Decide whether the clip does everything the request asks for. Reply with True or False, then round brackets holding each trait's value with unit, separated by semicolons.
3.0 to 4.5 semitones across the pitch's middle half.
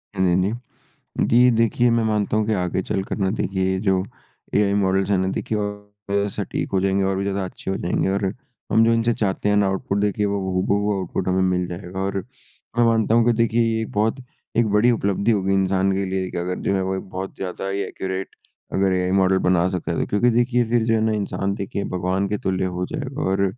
False (2.4 semitones)